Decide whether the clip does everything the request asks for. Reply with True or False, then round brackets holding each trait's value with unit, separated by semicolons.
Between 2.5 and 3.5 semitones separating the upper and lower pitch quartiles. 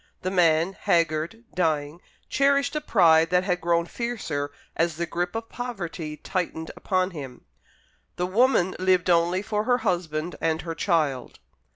True (3.1 semitones)